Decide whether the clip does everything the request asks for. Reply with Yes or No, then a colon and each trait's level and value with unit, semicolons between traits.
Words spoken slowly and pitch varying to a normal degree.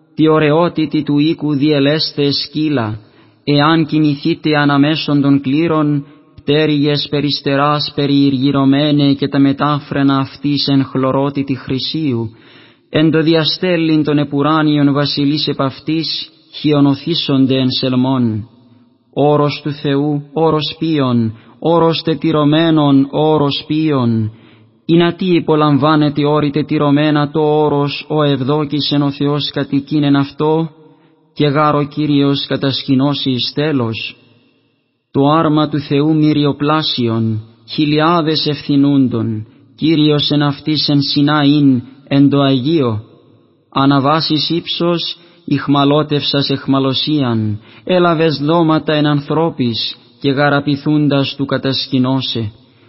No: slow, 105 wpm; narrow, 1.9 semitones